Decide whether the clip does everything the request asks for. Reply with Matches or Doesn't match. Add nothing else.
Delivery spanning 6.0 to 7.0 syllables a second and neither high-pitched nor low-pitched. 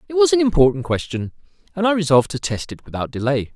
Matches